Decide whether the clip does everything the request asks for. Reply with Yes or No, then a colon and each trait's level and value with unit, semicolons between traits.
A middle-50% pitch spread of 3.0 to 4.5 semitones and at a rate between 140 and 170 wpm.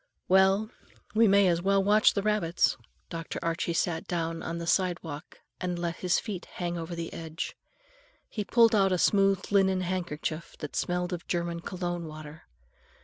No: narrow, 2.5 semitones; average, 165 wpm